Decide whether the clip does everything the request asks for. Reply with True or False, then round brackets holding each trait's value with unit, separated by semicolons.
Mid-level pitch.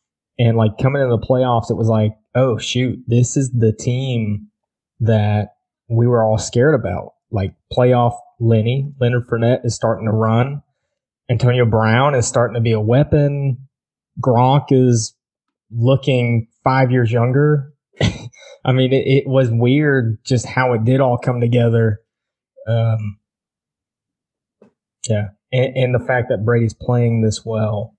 False (120 Hz)